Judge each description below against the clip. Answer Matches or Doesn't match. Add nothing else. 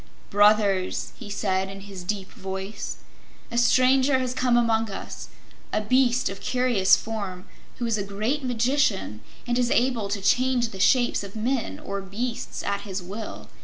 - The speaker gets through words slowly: Doesn't match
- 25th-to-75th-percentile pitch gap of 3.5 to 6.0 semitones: Matches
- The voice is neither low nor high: Doesn't match